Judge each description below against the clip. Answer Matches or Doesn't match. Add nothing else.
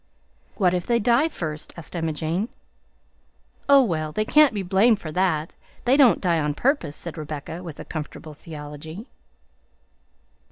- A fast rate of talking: Doesn't match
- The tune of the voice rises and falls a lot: Matches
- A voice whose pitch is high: Doesn't match